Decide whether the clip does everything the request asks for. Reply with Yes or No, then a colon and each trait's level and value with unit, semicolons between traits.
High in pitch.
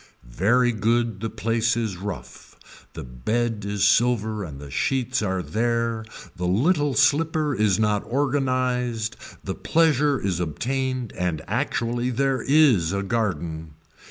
No: low, 115 Hz